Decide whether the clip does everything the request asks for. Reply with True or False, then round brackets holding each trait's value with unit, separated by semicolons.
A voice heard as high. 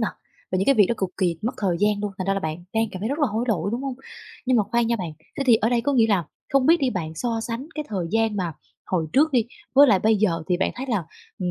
True (215 Hz)